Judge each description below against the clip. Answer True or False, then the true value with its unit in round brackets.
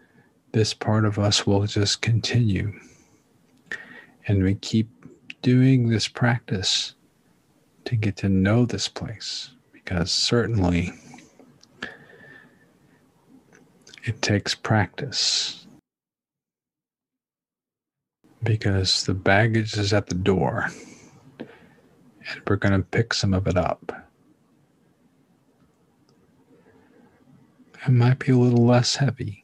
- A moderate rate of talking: False (95 wpm)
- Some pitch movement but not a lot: True (3.4 semitones)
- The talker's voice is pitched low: True (110 Hz)